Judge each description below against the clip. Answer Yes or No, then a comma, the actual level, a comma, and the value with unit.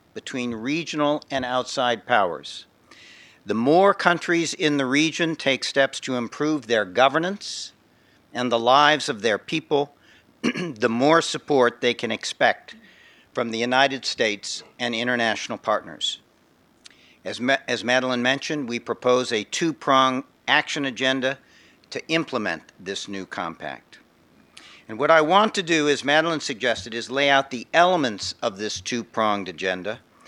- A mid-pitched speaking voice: No, low, 130 Hz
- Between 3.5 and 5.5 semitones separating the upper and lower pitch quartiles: Yes, average, 4.2 semitones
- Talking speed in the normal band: Yes, average, 145 wpm